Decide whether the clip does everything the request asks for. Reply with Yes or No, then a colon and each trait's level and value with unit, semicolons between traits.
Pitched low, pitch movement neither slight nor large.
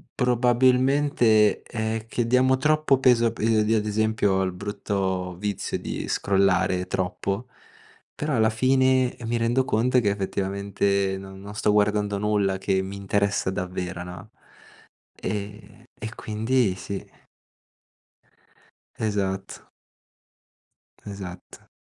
Yes: low, 105 Hz; average, 3.4 semitones